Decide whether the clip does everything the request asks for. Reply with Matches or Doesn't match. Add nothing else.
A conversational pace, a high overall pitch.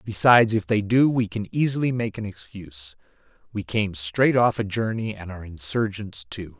Doesn't match